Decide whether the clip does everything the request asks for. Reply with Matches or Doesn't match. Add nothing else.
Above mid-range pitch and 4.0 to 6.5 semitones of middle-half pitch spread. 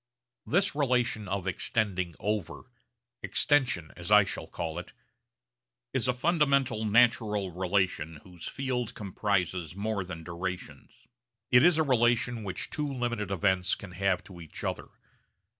Doesn't match